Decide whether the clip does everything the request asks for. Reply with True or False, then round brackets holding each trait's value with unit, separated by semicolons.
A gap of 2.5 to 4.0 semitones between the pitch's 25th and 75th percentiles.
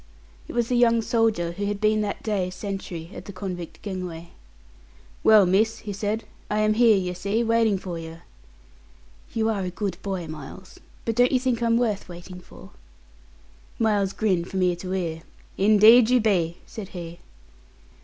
True (3.5 semitones)